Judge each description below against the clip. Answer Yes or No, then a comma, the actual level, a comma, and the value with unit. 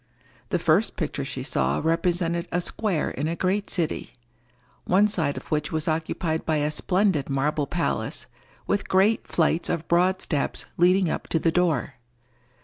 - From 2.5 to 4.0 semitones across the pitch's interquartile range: Yes, average, 2.9 semitones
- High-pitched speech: No, medium, 170 Hz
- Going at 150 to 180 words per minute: Yes, average, 160 wpm